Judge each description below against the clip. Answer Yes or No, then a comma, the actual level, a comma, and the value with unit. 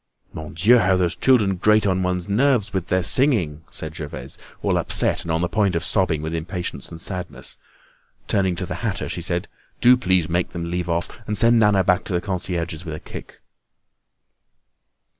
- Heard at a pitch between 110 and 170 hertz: No, very low, 90 Hz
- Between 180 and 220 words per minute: Yes, average, 190 wpm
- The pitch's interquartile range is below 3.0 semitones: No, average, 3.4 semitones